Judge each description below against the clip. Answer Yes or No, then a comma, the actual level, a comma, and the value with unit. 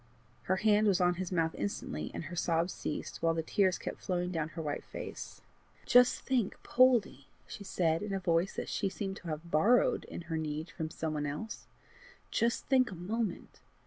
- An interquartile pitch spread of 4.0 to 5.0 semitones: Yes, average, 4.4 semitones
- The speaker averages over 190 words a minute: Yes, average, 200 wpm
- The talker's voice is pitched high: No, medium, 180 Hz